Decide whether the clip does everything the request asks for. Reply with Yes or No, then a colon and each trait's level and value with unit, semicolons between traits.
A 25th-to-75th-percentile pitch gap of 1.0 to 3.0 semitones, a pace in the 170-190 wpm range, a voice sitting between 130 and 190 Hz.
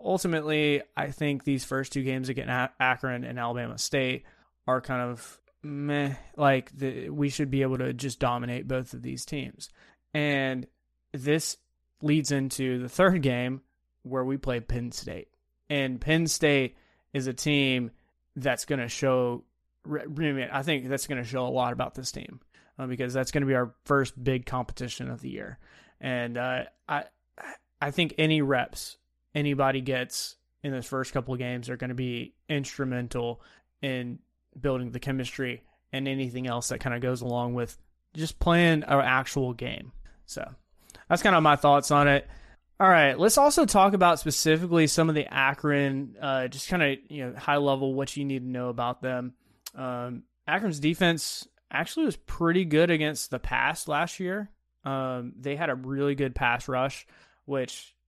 Yes: average, 2.7 semitones; average, 175 wpm; low, 135 Hz